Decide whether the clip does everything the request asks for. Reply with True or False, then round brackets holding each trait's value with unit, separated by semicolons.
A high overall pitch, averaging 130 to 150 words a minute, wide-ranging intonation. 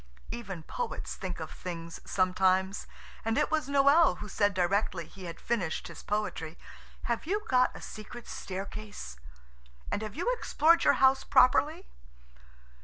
True (210 Hz; 145 wpm; 6.7 semitones)